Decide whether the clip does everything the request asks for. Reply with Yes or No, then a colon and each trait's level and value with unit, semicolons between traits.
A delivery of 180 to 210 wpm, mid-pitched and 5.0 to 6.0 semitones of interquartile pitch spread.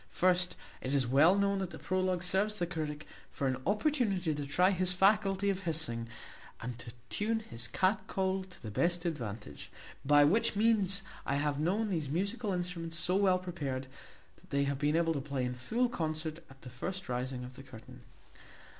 Yes: average, 190 wpm; medium, 170 Hz; wide, 5.5 semitones